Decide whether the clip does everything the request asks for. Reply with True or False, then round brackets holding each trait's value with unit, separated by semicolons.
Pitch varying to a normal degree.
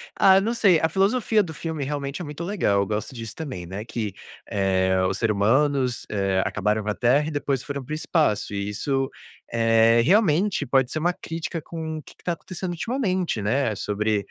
False (7.6 semitones)